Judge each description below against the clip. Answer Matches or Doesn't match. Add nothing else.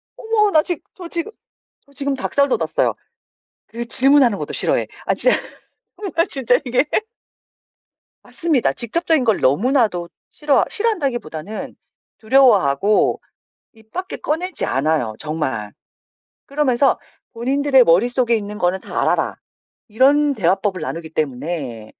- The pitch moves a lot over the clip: Matches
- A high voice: Matches